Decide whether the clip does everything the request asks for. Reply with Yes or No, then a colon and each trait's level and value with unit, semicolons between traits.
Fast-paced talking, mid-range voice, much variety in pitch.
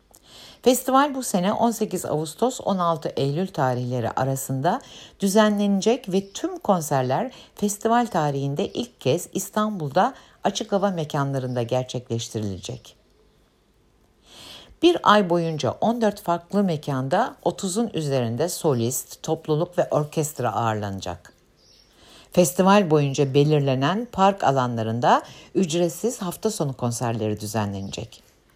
No: slow, 95 wpm; medium, 160 Hz; wide, 7.8 semitones